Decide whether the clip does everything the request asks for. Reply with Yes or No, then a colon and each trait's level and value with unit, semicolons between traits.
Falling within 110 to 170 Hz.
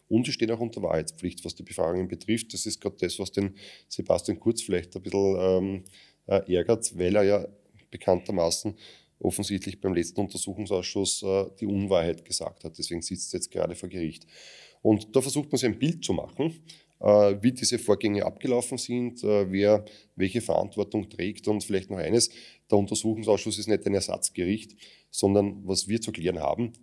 No: low, 100 Hz